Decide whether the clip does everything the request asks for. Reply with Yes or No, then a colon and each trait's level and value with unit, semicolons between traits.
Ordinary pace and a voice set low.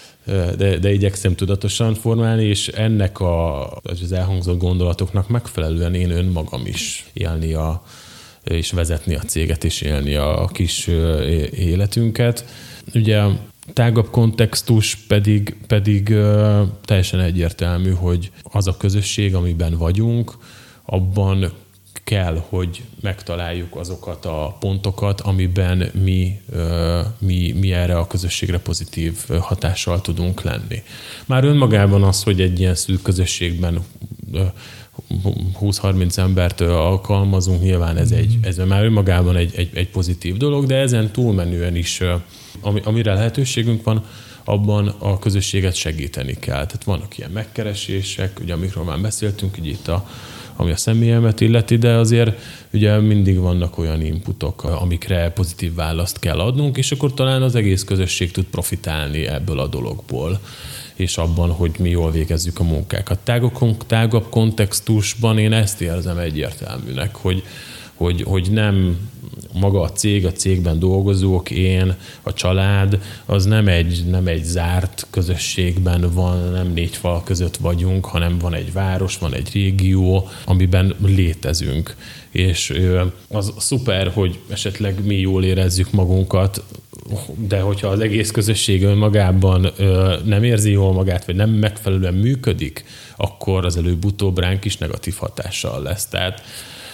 Yes: average, 130 wpm; very low, 95 Hz